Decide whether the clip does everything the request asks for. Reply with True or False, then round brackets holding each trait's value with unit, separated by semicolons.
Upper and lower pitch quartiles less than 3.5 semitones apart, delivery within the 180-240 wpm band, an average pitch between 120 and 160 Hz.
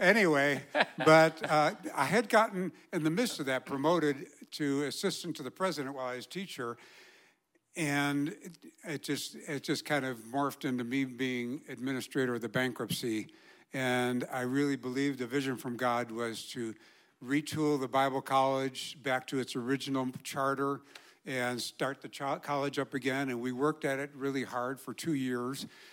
False (2.9 semitones; 165 wpm; 140 Hz)